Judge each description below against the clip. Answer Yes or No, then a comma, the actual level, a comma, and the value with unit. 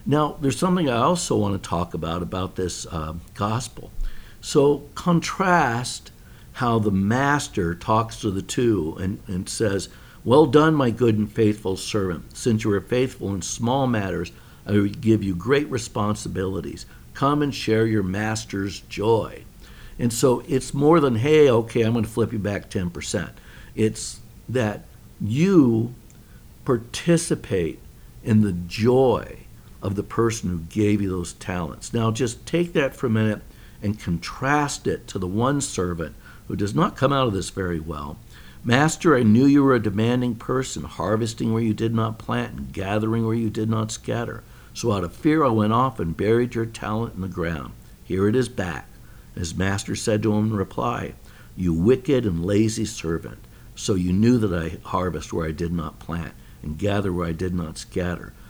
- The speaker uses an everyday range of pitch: Yes, average, 4.4 semitones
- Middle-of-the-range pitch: No, low, 110 Hz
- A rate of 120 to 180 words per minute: Yes, average, 175 wpm